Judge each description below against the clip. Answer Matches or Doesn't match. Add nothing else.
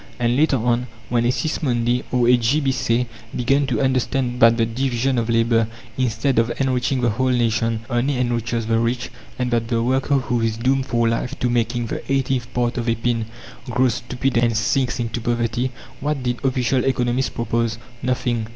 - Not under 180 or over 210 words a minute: Matches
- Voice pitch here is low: Matches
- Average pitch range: Doesn't match